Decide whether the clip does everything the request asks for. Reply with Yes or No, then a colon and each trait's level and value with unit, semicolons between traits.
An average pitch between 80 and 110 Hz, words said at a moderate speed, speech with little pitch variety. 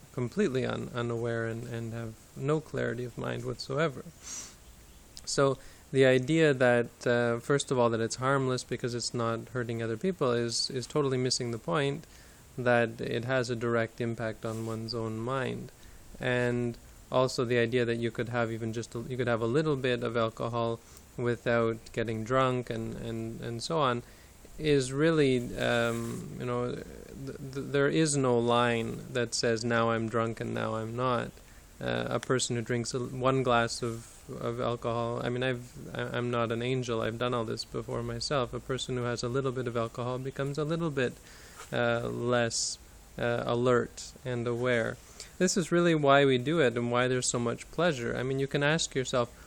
No: low, 120 Hz; average, 185 wpm; narrow, 2.0 semitones